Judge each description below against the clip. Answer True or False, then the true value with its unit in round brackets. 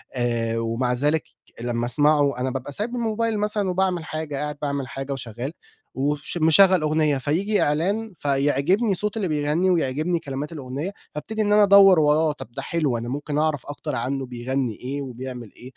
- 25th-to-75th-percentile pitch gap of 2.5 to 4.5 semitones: False (5.3 semitones)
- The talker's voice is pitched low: False (145 Hz)